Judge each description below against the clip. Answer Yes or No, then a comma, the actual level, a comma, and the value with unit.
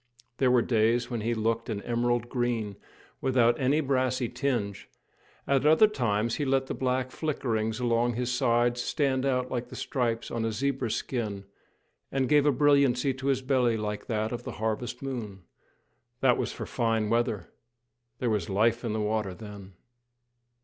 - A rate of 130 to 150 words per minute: No, average, 170 wpm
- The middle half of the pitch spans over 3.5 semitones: No, average, 2.8 semitones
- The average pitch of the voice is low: Yes, low, 120 Hz